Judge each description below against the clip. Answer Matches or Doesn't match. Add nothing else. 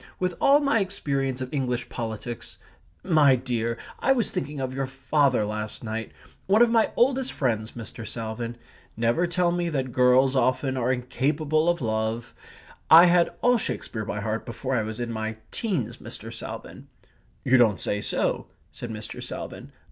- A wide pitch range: Matches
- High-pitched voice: Doesn't match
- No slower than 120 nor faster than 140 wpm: Doesn't match